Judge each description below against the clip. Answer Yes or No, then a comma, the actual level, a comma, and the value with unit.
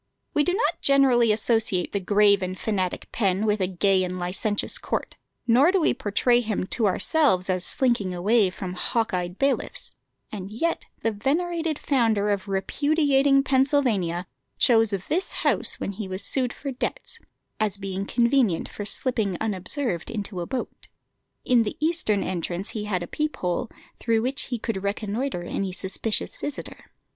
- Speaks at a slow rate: No, average, 160 wpm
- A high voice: Yes, high, 215 Hz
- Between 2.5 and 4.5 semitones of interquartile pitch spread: No, wide, 5.5 semitones